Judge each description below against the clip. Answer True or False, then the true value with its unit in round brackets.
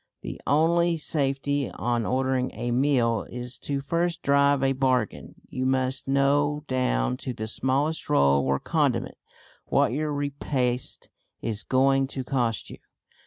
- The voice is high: False (135 Hz)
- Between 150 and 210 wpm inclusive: False (140 wpm)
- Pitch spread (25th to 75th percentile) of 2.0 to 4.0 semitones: True (2.6 semitones)